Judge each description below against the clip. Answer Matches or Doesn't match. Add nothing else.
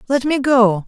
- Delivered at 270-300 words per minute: Doesn't match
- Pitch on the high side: Matches